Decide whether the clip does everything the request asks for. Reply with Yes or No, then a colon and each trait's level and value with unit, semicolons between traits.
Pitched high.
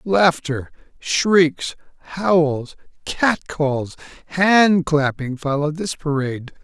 No: medium, 160 Hz